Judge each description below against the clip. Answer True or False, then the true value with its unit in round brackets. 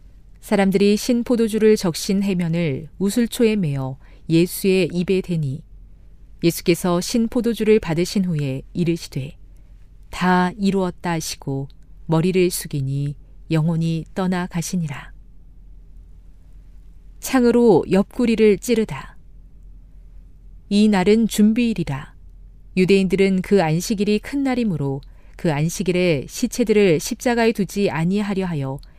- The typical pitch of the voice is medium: True (175 Hz)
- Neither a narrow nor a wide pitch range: False (6.8 semitones)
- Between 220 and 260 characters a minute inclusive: True (255 characters per minute)